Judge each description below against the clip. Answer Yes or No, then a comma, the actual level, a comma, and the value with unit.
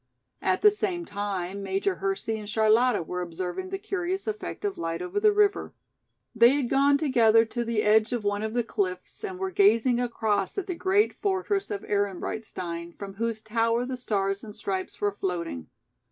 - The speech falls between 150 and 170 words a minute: No, average, 180 wpm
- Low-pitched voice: No, high, 225 Hz